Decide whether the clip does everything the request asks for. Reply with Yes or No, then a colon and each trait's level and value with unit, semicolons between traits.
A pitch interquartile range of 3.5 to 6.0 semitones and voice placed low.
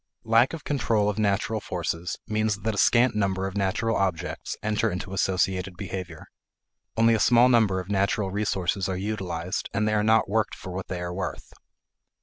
No: average, 2.7 semitones; low, 100 Hz